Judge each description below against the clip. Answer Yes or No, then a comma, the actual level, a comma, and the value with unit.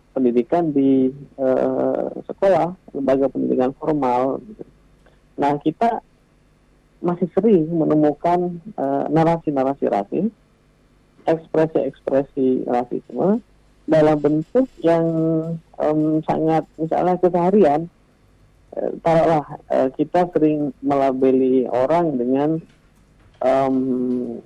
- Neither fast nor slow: No, slow, 80 wpm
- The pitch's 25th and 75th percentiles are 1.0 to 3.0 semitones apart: No, average, 3.8 semitones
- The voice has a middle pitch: Yes, medium, 150 Hz